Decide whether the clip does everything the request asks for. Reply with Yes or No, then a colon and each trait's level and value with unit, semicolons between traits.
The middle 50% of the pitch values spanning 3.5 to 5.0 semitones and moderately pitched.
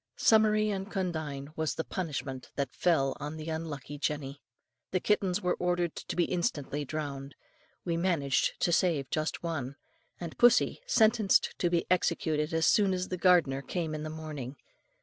Yes: average, 3.8 semitones; medium, 160 Hz